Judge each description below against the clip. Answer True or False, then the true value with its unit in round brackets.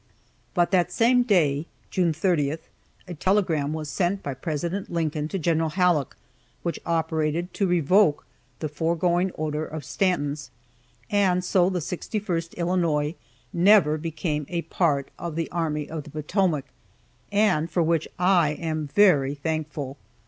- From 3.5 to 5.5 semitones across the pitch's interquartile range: False (3.0 semitones)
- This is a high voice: False (165 Hz)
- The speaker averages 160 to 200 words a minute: False (140 wpm)